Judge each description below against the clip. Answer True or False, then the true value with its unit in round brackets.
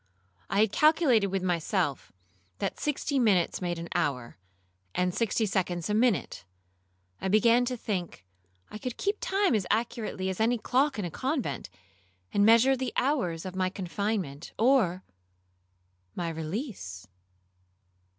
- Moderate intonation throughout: False (6.1 semitones)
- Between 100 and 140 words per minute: True (135 wpm)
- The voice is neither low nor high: False (195 Hz)